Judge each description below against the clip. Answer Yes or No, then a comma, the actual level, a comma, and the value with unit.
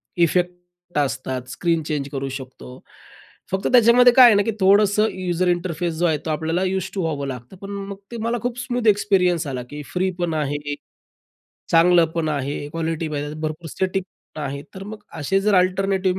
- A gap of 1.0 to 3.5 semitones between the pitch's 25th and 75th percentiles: No, average, 4.3 semitones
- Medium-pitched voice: Yes, medium, 175 Hz